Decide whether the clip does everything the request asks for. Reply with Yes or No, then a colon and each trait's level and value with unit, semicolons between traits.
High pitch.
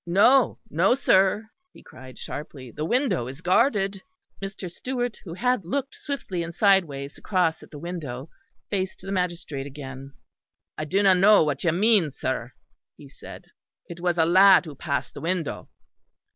No: medium, 180 Hz